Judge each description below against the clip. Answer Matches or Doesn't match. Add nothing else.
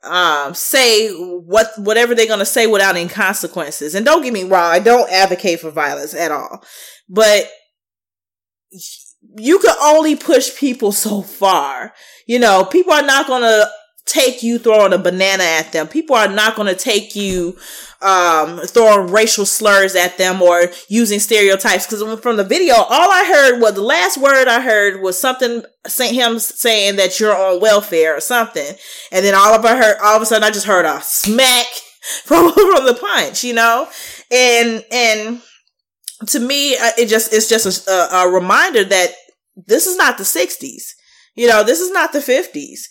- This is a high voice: Matches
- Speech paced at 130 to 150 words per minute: Doesn't match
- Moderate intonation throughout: Matches